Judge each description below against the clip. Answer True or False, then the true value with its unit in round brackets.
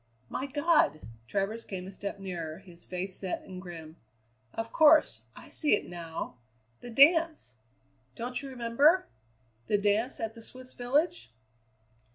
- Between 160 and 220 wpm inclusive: False (145 wpm)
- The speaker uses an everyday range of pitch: False (6.6 semitones)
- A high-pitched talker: True (220 Hz)